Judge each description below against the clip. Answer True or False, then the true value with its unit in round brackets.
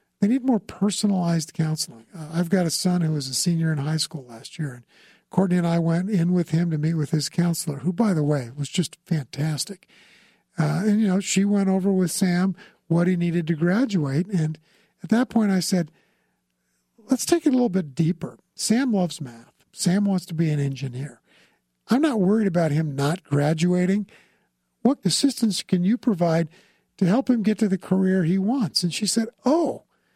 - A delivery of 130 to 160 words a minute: False (200 wpm)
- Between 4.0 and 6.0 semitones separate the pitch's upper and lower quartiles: True (4.3 semitones)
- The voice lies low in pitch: False (180 Hz)